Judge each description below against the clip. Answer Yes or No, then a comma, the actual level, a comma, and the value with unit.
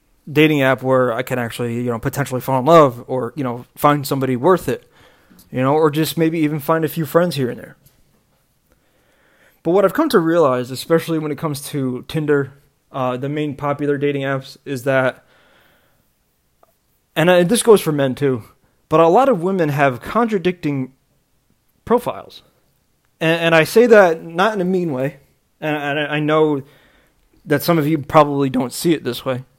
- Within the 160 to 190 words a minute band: Yes, average, 185 wpm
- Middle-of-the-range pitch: Yes, medium, 145 Hz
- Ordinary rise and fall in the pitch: Yes, average, 3.6 semitones